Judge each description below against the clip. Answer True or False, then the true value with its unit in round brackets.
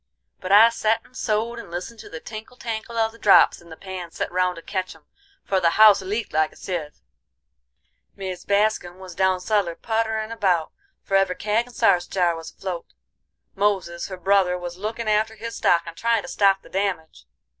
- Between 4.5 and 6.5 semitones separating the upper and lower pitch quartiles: False (3.6 semitones)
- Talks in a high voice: True (195 Hz)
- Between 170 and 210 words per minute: True (200 wpm)